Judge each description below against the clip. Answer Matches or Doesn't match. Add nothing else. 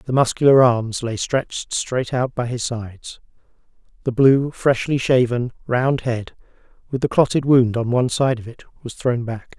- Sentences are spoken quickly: Doesn't match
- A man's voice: Matches